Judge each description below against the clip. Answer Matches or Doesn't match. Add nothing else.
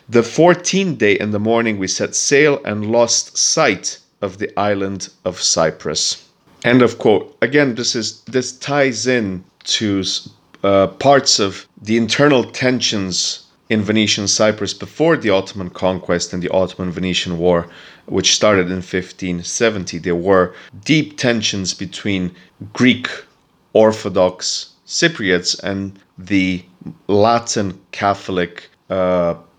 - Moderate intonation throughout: Matches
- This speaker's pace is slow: Matches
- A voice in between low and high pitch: Doesn't match